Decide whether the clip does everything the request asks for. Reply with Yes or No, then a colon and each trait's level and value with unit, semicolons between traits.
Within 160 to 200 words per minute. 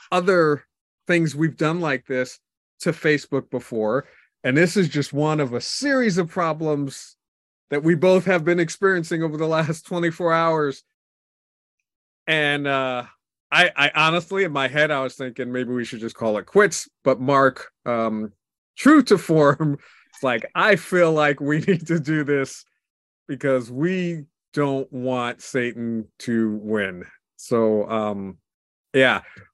No: average, 150 wpm